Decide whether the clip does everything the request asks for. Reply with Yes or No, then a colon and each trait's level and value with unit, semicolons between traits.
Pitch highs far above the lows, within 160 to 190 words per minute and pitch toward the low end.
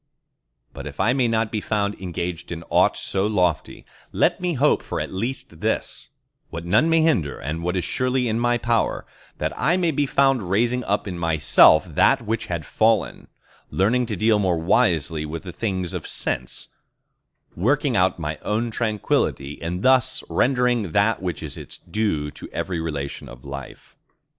Yes: wide, 6.3 semitones; average, 165 wpm; low, 100 Hz